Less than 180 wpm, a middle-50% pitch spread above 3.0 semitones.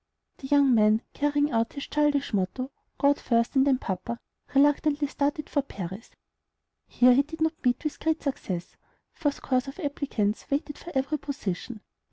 Yes: average, 165 wpm; average, 3.9 semitones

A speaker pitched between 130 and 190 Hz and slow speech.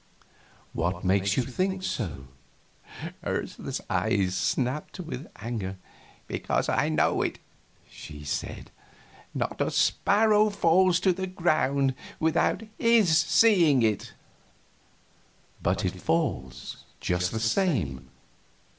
Yes: low, 135 Hz; slow, 105 wpm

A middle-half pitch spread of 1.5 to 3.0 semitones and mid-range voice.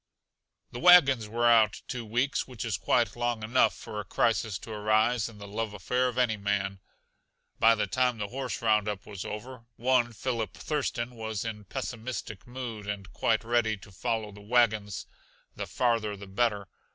No: narrow, 2.6 semitones; low, 115 Hz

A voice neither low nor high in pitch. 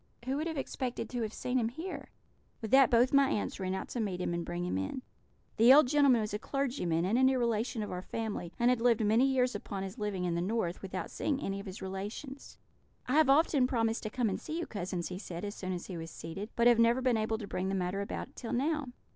No: high, 225 Hz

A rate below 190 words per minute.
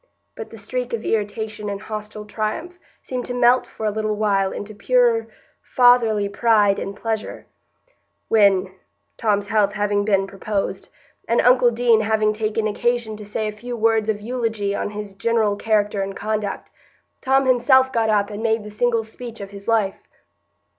Yes: average, 165 wpm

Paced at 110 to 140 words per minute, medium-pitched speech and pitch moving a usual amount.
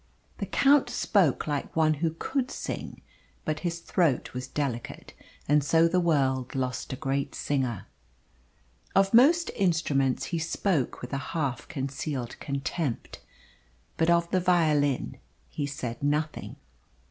Yes: slow, 135 wpm; medium, 150 Hz; average, 4.0 semitones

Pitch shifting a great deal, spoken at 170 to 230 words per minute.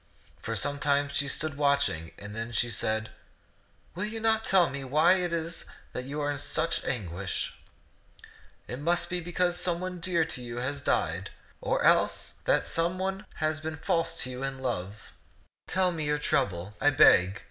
Yes: wide, 5.7 semitones; average, 180 wpm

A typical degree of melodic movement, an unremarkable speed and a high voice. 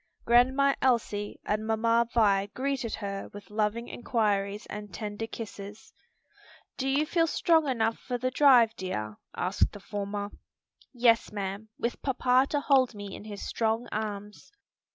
Yes: average, 3.4 semitones; average, 145 wpm; high, 220 Hz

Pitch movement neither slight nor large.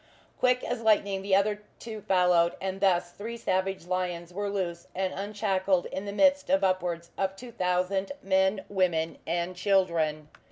No: narrow, 2.3 semitones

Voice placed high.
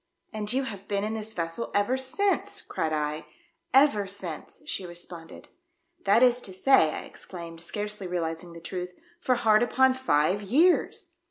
Yes: high, 205 Hz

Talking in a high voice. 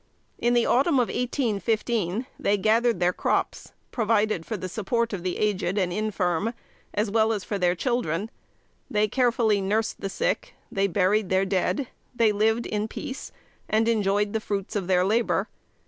Yes: high, 210 Hz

